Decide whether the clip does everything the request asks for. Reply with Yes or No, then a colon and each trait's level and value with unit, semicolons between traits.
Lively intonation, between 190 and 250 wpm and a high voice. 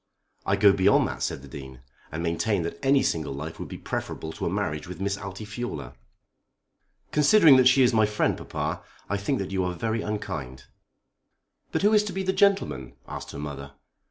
No: wide, 7.6 semitones; average, 195 wpm; low, 100 Hz